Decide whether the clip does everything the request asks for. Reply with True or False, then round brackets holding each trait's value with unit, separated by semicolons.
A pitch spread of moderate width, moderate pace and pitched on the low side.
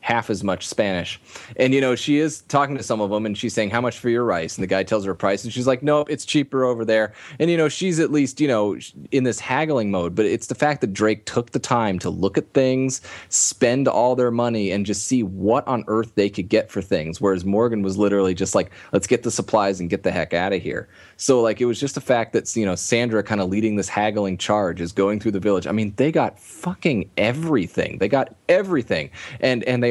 False (4.5 semitones; 255 wpm; 115 Hz)